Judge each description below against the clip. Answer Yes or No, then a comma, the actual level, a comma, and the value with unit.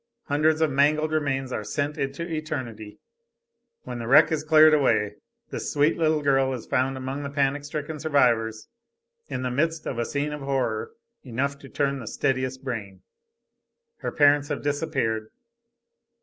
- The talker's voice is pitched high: No, medium, 140 Hz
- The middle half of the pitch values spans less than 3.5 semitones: Yes, average, 2.8 semitones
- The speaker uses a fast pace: No, average, 160 wpm